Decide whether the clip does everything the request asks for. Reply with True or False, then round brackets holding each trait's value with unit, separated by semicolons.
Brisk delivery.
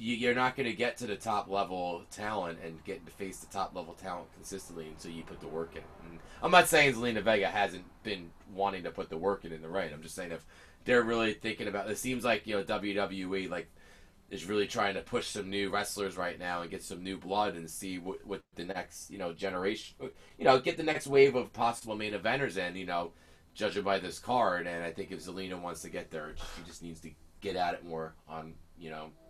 True (240 wpm)